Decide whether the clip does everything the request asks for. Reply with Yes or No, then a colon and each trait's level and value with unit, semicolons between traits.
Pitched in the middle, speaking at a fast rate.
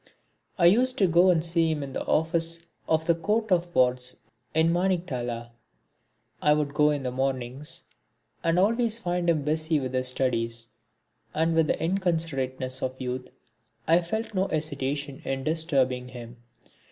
No: medium, 155 Hz; average, 155 wpm